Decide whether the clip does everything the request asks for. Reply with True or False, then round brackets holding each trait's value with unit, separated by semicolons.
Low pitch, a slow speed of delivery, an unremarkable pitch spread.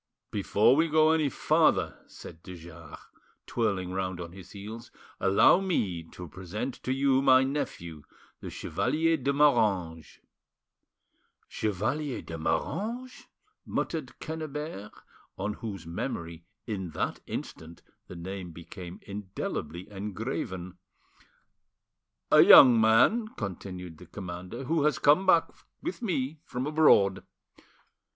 False (105 Hz; 115 wpm; 7.8 semitones)